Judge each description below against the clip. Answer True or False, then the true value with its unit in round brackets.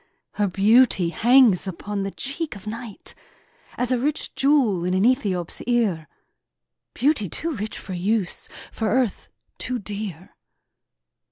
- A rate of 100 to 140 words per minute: True (135 wpm)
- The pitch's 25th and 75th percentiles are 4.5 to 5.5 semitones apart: True (4.8 semitones)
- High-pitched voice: True (215 Hz)